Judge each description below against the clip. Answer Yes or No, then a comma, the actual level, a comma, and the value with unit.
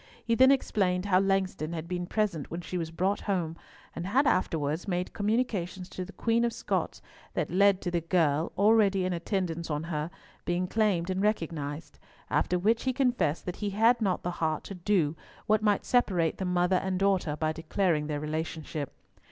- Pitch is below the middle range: No, medium, 180 Hz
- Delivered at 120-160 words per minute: No, average, 185 wpm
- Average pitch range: Yes, average, 3.6 semitones